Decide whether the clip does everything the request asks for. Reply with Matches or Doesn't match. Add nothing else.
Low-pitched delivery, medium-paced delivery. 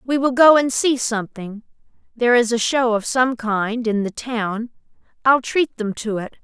Doesn't match